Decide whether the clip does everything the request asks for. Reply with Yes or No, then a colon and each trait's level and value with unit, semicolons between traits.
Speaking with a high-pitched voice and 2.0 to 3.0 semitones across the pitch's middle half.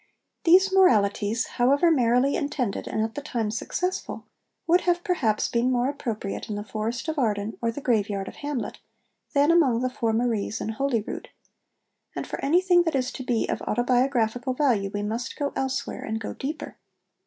No: high, 245 Hz; average, 4.5 semitones